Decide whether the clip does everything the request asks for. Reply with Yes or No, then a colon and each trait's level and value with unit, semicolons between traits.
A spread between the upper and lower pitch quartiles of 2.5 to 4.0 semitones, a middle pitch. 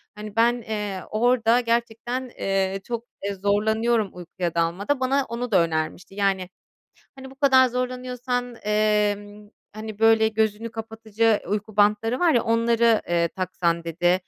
No: average, 3.2 semitones; high, 220 Hz